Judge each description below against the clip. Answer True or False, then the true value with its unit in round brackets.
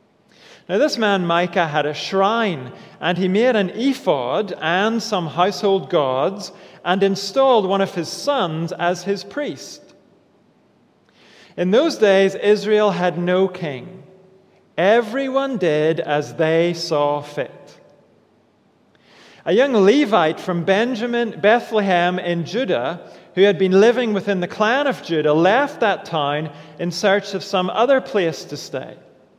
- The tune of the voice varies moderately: True (3.7 semitones)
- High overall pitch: True (195 Hz)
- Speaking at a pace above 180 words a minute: False (135 wpm)